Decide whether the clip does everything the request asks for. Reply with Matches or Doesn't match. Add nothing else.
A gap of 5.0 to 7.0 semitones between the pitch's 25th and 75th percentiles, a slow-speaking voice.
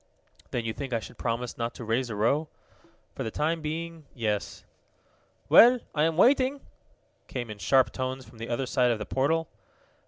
Doesn't match